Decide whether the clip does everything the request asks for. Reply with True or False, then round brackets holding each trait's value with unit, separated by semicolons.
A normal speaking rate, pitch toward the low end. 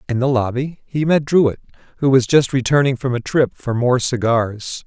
True (195 wpm; 130 Hz)